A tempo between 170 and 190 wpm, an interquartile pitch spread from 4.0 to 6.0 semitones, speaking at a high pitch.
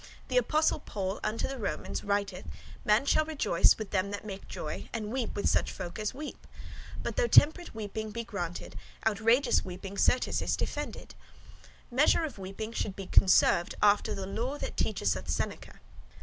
Yes: average, 175 wpm; average, 4.4 semitones; high, 215 Hz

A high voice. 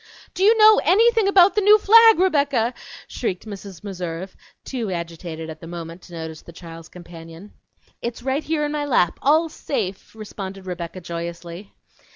Yes: high, 195 Hz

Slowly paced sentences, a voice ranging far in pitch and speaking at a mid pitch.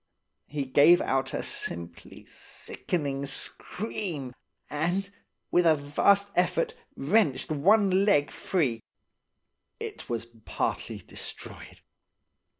Yes: slow, 95 wpm; wide, 6.1 semitones; medium, 155 Hz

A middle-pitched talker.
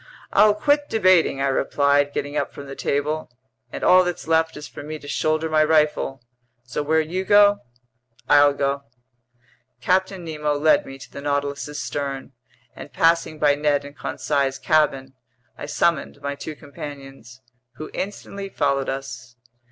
Yes: medium, 145 Hz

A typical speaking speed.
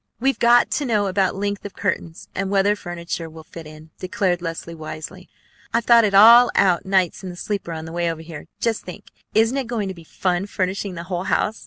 No: fast, 220 wpm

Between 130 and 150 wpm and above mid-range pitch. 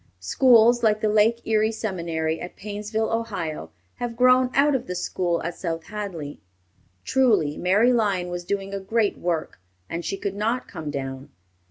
No: average, 165 wpm; high, 200 Hz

